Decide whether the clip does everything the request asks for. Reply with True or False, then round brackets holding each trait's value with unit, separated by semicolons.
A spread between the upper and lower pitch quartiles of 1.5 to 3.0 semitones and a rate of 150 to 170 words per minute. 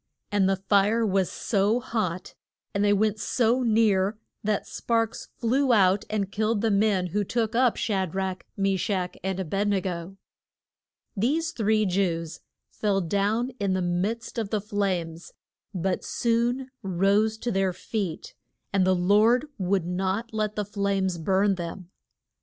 True (2.7 semitones; 155 wpm)